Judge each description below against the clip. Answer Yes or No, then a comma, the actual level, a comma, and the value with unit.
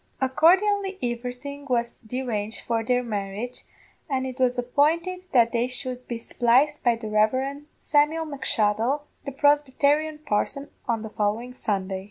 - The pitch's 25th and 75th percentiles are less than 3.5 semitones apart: No, average, 3.8 semitones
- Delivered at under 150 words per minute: Yes, average, 140 wpm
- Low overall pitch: No, very high, 250 Hz